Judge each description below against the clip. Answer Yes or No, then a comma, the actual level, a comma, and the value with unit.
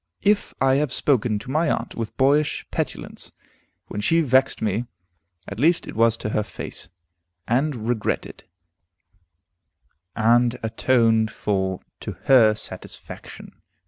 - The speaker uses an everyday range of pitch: Yes, average, 3.7 semitones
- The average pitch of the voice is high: No, low, 120 Hz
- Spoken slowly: Yes, slow, 125 wpm